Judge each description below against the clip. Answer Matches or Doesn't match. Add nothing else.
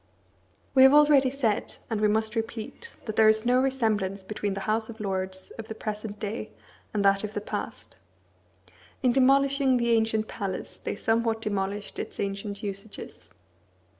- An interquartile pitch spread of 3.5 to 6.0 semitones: Doesn't match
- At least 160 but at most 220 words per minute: Matches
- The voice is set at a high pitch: Matches